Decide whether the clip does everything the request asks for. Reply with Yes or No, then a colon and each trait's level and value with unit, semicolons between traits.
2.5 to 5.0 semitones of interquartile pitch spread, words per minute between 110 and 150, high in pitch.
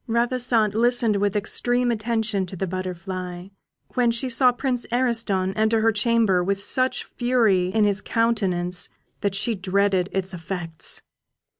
Yes: average, 3.9 semitones; average, 140 wpm; high, 210 Hz